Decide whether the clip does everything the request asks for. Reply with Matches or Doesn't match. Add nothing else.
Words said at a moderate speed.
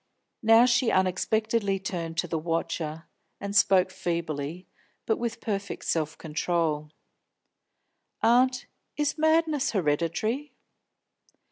Doesn't match